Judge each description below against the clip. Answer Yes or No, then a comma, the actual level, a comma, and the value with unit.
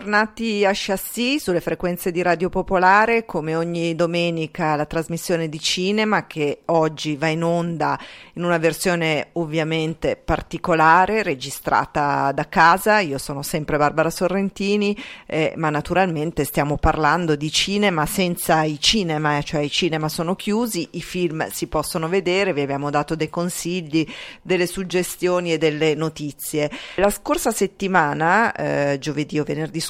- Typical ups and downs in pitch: Yes, average, 3.3 semitones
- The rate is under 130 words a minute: No, average, 145 wpm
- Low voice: No, medium, 170 Hz